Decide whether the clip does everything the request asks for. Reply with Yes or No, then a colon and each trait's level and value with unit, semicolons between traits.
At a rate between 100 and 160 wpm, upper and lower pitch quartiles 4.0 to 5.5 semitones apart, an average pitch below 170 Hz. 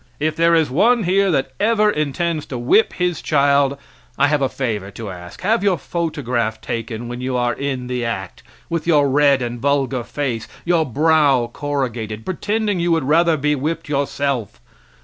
No: average, 175 wpm; average, 5.2 semitones; medium, 140 Hz